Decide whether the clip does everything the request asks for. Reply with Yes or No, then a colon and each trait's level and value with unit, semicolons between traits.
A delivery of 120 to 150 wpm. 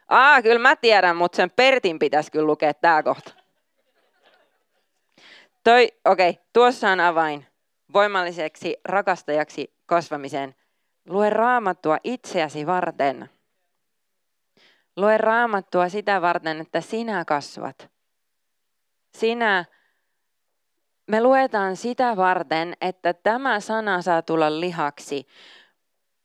No: slow, 95 wpm